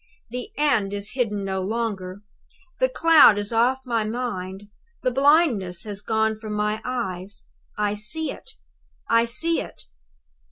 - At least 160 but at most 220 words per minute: No, average, 145 wpm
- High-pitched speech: Yes, high, 220 Hz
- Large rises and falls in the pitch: No, average, 3.7 semitones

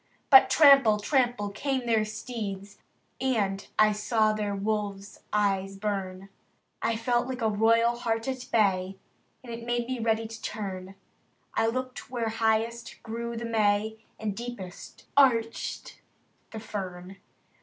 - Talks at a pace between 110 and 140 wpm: Yes, slow, 135 wpm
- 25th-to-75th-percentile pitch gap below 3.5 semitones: Yes, narrow, 2.5 semitones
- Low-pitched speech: No, high, 220 Hz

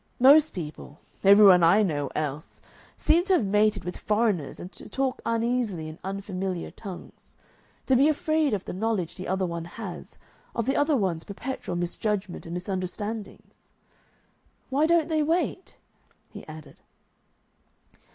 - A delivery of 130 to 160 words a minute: Yes, average, 145 wpm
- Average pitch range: No, wide, 6.5 semitones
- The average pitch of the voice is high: Yes, high, 200 Hz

